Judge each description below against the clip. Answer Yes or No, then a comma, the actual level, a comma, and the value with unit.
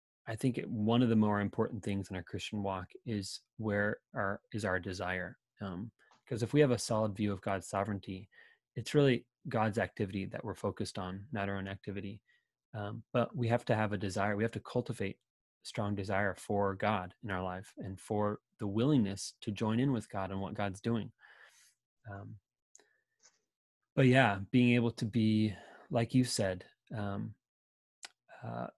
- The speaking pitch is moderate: No, low, 105 Hz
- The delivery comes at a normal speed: Yes, average, 180 wpm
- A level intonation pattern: No, average, 3.1 semitones